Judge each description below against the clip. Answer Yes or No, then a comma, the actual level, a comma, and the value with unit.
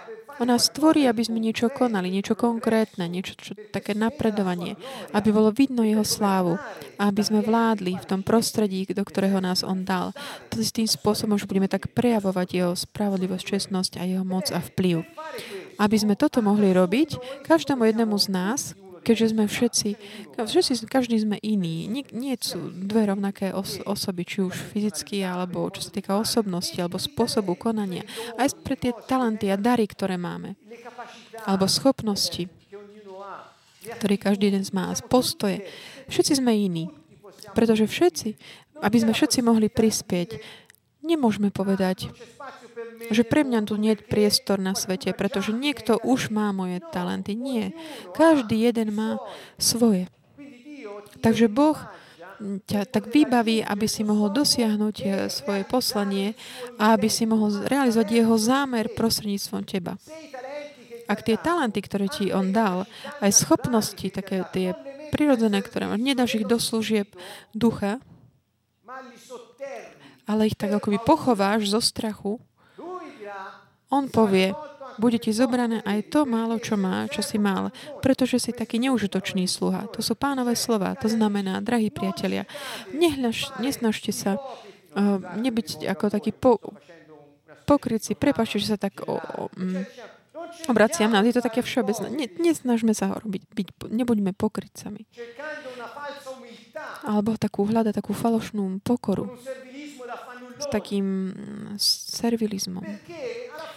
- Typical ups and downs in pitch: Yes, average, 3.4 semitones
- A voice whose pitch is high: Yes, high, 215 Hz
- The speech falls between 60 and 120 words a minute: No, average, 135 wpm